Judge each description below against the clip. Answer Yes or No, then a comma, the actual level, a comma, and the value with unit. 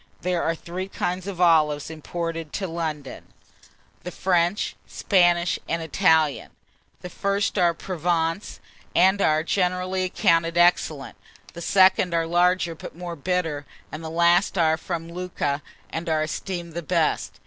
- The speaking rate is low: No, average, 145 wpm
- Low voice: No, medium, 170 Hz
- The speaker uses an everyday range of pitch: No, narrow, 1.9 semitones